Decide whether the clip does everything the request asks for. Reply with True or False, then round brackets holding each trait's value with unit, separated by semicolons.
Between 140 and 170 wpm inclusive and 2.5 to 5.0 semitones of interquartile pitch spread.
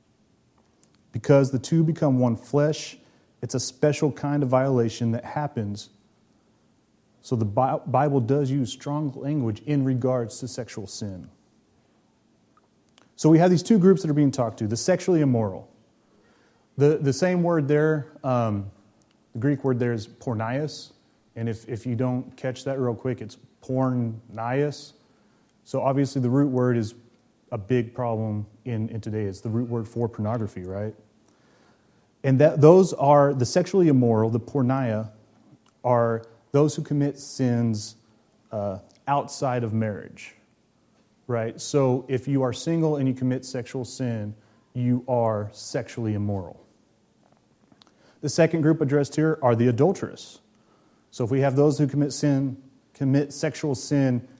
True (150 wpm; 4.0 semitones)